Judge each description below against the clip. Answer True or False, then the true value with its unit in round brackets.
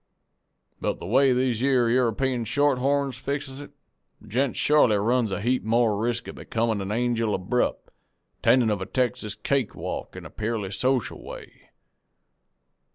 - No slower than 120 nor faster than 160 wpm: True (155 wpm)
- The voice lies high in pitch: False (120 Hz)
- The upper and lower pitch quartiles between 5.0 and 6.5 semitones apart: False (3.2 semitones)